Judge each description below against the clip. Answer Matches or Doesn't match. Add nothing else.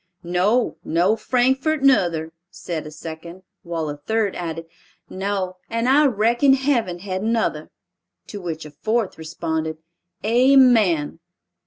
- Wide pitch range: Matches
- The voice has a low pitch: Doesn't match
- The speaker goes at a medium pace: Doesn't match